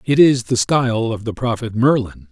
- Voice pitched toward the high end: No, low, 120 Hz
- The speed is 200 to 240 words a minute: Yes, fast, 205 wpm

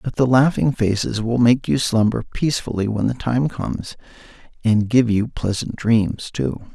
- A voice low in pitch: Yes, low, 115 Hz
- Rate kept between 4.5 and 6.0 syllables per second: Yes, 4.7 syllables/s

